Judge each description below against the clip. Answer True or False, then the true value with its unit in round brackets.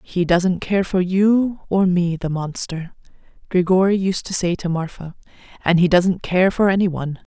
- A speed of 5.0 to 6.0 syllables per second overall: False (4.6 syllables/s)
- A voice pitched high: False (180 Hz)